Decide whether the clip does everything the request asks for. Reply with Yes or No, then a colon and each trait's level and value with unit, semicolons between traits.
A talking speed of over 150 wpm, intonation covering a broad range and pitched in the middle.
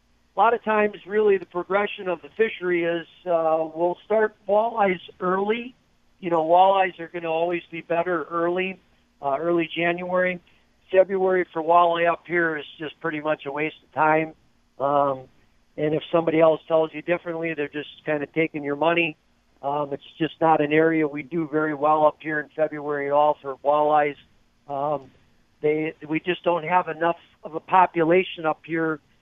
No: average, 180 wpm; average, 2.8 semitones; medium, 160 Hz